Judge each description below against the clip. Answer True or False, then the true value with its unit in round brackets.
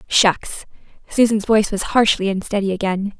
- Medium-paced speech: False (130 wpm)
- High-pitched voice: True (205 Hz)